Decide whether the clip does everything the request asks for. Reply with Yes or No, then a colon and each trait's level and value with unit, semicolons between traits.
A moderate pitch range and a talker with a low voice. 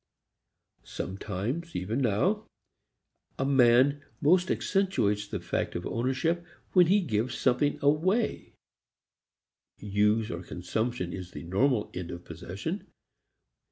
No: wide, 8.0 semitones; low, 120 Hz